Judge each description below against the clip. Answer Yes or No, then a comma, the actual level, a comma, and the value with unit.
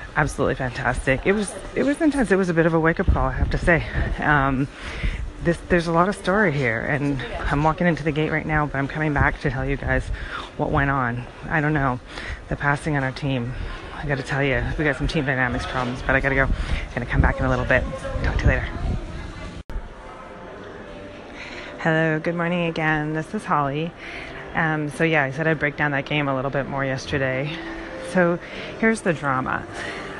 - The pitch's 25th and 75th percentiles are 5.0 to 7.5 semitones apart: No, average, 3.7 semitones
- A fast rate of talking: Yes, fast, 210 wpm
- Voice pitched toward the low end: No, medium, 145 Hz